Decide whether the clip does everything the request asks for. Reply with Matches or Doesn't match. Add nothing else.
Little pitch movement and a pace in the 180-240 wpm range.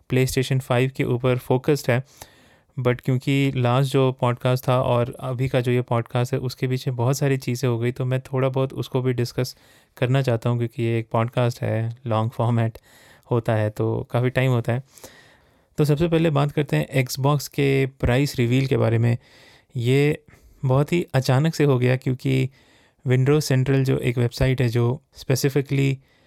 Matches